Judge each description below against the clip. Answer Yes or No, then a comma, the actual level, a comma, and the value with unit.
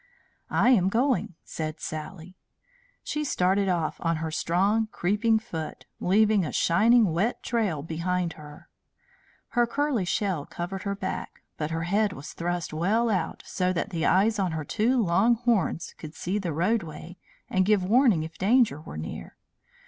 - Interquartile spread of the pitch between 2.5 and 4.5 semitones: No, average, 4.9 semitones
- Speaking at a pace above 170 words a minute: No, average, 160 wpm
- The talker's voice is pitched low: No, medium, 185 Hz